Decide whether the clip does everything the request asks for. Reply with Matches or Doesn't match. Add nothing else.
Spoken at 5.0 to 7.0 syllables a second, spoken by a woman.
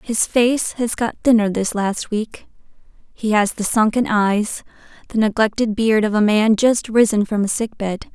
Doesn't match